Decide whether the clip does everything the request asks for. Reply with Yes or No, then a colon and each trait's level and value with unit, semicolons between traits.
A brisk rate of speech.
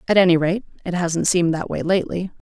Yes: fast, 215 wpm